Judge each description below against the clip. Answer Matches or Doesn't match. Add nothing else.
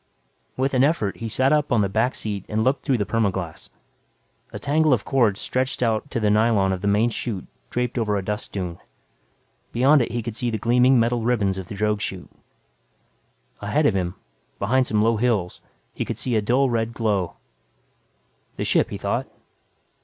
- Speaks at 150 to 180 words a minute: Doesn't match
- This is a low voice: Matches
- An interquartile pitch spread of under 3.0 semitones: Doesn't match